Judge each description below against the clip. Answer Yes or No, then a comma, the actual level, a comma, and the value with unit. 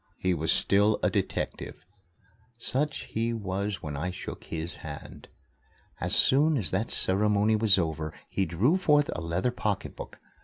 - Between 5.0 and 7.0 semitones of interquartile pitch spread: Yes, average, 5.3 semitones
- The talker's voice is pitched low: Yes, low, 100 Hz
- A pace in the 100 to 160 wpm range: Yes, average, 150 wpm